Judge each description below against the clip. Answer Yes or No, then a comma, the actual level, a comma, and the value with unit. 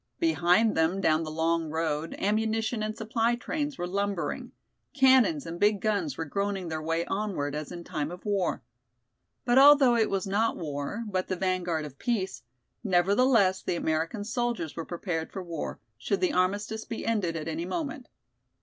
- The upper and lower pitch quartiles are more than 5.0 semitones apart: Yes, wide, 5.4 semitones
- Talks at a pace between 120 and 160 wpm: No, average, 170 wpm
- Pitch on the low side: No, high, 195 Hz